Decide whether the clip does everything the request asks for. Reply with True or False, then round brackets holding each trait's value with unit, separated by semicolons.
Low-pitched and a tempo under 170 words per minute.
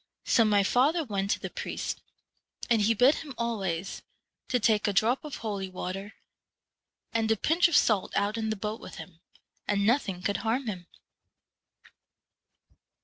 False (215 Hz; 160 wpm)